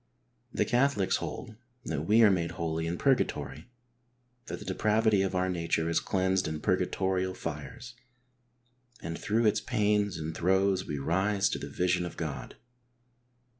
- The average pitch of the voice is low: Yes, very low, 95 Hz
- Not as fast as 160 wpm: Yes, average, 150 wpm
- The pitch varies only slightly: No, average, 3.9 semitones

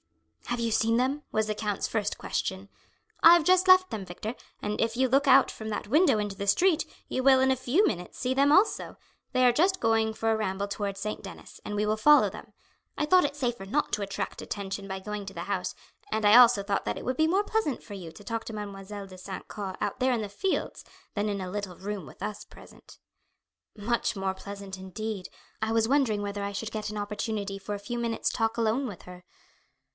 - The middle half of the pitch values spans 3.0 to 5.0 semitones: Yes, average, 4.1 semitones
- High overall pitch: Yes, high, 215 Hz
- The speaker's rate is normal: No, fast, 230 wpm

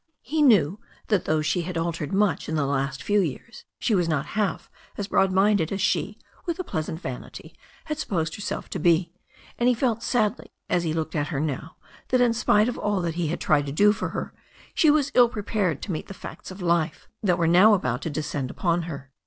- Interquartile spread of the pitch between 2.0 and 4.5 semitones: No, average, 5.1 semitones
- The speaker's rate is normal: No, fast, 225 wpm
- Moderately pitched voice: Yes, medium, 175 Hz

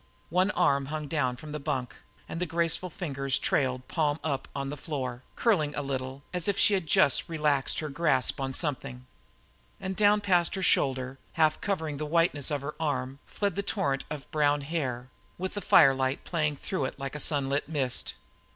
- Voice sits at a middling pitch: Yes, medium, 150 Hz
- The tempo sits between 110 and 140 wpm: No, average, 190 wpm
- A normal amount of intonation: Yes, average, 3.6 semitones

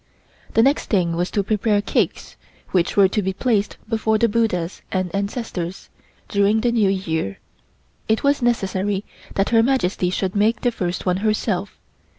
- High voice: Yes, high, 205 Hz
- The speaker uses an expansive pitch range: No, average, 3.2 semitones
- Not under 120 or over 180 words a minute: Yes, average, 160 wpm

